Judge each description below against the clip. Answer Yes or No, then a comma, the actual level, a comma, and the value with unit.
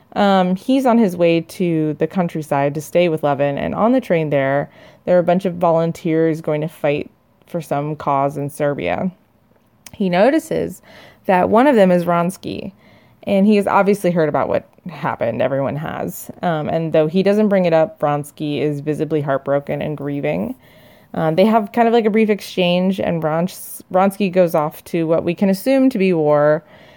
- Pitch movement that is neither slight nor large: Yes, average, 4.5 semitones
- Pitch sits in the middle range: Yes, medium, 170 Hz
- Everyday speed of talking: Yes, average, 195 wpm